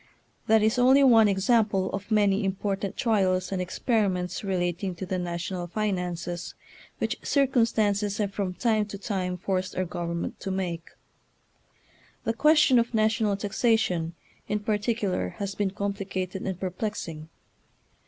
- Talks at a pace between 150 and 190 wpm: No, slow, 135 wpm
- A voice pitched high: Yes, high, 195 Hz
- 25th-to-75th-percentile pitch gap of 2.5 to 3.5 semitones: Yes, average, 2.9 semitones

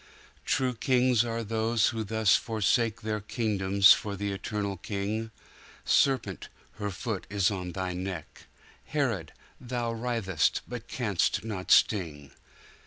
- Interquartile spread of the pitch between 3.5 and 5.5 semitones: No, average, 3.1 semitones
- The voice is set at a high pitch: No, low, 105 Hz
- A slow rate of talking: Yes, slow, 120 wpm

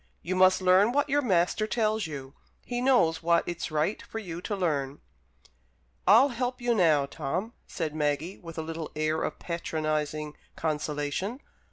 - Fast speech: No, average, 160 wpm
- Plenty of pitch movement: Yes, wide, 5.8 semitones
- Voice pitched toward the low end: No, medium, 170 Hz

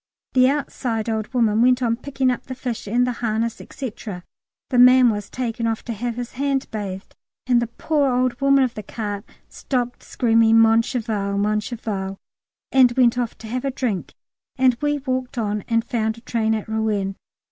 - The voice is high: Yes, high, 235 Hz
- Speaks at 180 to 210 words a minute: Yes, average, 190 wpm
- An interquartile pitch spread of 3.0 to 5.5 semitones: No, narrow, 2.5 semitones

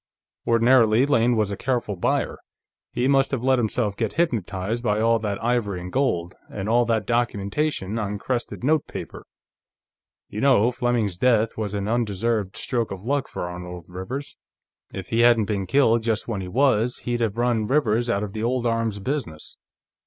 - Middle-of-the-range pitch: No, low, 115 Hz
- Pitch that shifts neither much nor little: Yes, average, 3.2 semitones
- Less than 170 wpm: No, average, 175 wpm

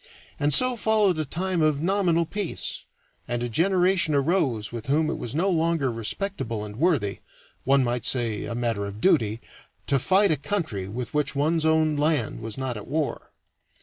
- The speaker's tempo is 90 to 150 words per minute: No, average, 180 wpm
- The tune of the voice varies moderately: No, wide, 6.2 semitones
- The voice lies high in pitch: No, medium, 150 Hz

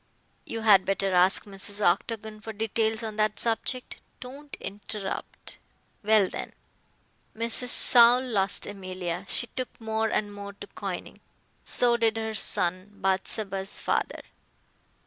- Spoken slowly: Yes, slow, 125 wpm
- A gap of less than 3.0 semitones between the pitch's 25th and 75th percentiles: Yes, narrow, 2.5 semitones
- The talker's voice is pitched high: Yes, high, 215 Hz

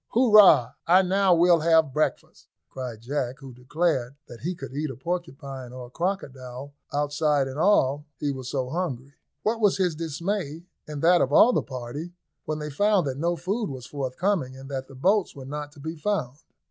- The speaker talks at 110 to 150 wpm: No, average, 190 wpm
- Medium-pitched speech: Yes, medium, 150 Hz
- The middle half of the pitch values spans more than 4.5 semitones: Yes, average, 5.0 semitones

